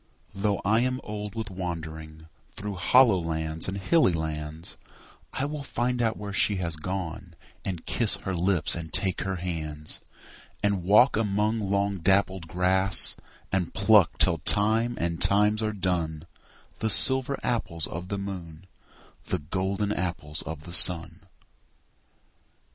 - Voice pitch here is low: Yes, very low, 95 Hz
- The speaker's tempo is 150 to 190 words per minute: No, average, 140 wpm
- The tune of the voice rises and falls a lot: No, average, 3.8 semitones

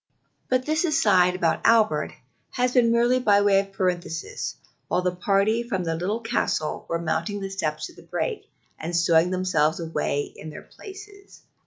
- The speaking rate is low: No, average, 170 wpm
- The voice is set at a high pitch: Yes, high, 195 Hz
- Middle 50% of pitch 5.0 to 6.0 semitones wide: Yes, wide, 5.6 semitones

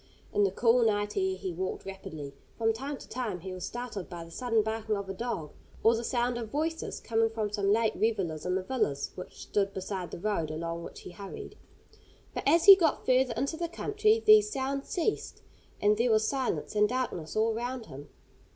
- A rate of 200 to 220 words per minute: Yes, fast, 205 wpm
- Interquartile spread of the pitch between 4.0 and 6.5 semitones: Yes, average, 5.0 semitones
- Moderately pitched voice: No, high, 220 Hz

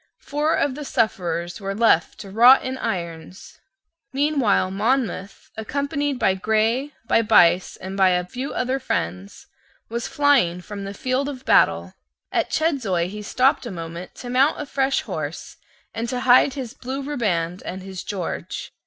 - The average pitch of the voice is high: Yes, high, 220 Hz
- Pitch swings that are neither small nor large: No, wide, 6.4 semitones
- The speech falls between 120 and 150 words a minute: No, average, 160 wpm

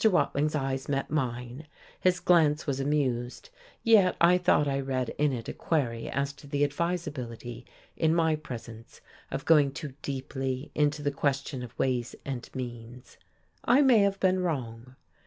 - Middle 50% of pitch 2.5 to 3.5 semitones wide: No, average, 3.9 semitones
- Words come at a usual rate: Yes, average, 155 wpm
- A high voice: No, medium, 140 Hz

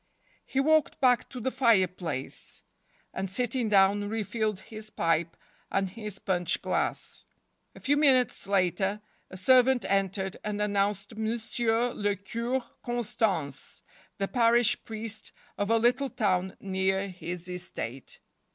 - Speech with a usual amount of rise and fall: Yes, average, 3.8 semitones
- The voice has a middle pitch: No, high, 210 Hz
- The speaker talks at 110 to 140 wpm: Yes, slow, 135 wpm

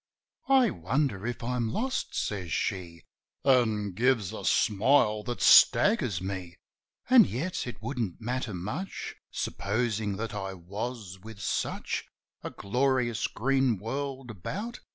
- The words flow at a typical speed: No, slow, 125 wpm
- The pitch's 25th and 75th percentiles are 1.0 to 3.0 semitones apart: No, average, 5.0 semitones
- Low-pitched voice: Yes, low, 115 Hz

